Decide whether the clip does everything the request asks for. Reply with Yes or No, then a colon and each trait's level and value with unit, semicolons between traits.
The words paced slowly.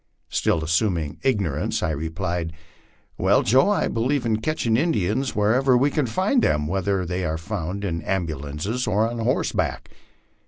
No: average, 150 wpm